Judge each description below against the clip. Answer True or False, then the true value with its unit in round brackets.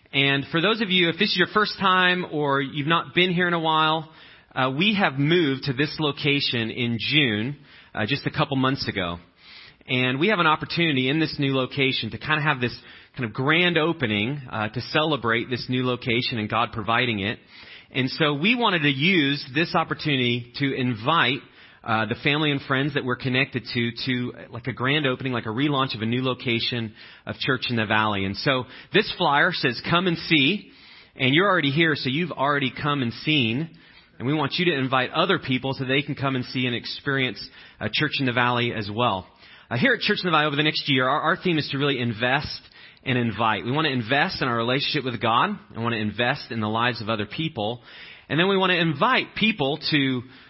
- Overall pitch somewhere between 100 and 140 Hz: True (135 Hz)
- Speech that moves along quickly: True (220 wpm)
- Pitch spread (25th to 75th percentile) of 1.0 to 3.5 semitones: False (4.3 semitones)